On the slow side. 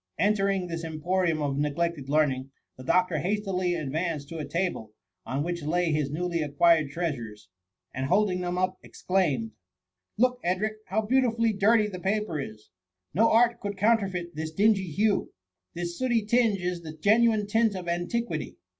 No: average, 170 wpm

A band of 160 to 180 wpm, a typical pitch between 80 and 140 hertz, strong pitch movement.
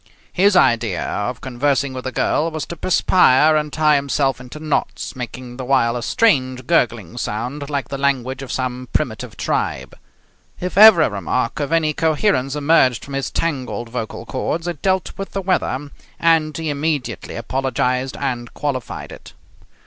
No: average, 165 wpm; low, 135 Hz; average, 3.8 semitones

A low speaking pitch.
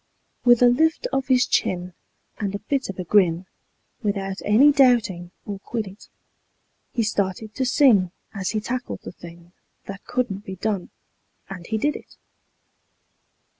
No: high, 210 Hz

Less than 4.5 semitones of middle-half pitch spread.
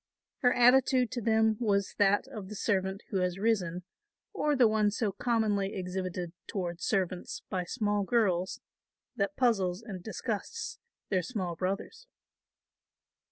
Yes: average, 3.6 semitones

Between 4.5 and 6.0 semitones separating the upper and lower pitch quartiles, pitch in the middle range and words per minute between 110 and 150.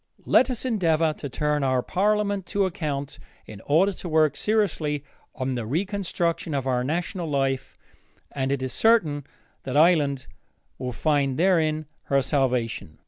Yes: average, 4.9 semitones; medium, 150 Hz; average, 145 wpm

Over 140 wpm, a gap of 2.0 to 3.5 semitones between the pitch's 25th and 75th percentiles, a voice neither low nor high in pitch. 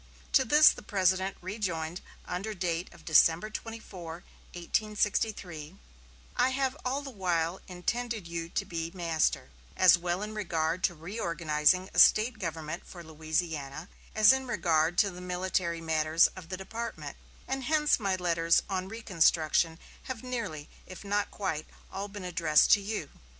No: average, 150 wpm; average, 4.3 semitones; medium, 180 Hz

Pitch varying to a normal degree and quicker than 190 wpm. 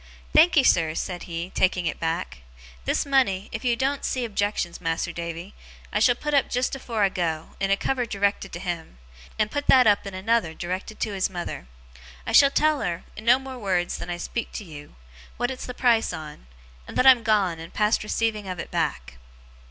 No: wide, 5.8 semitones; fast, 205 wpm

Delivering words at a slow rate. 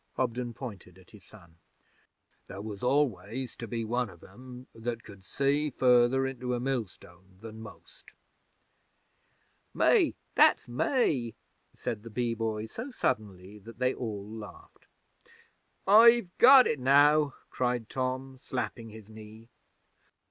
Yes: slow, 130 wpm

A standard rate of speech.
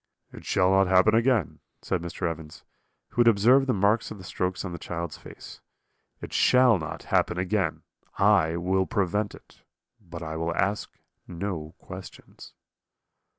Yes: average, 155 wpm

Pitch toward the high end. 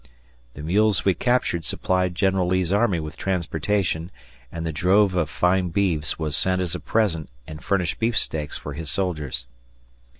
No: very low, 90 Hz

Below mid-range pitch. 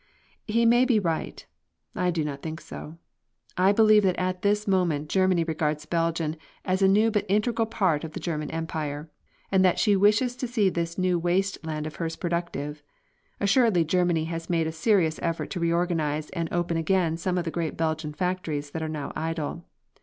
No: medium, 170 Hz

